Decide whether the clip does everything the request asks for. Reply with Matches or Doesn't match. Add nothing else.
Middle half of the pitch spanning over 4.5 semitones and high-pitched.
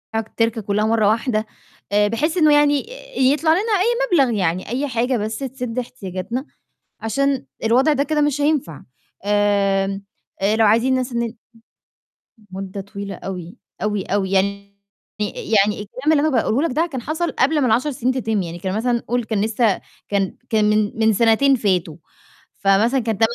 Matches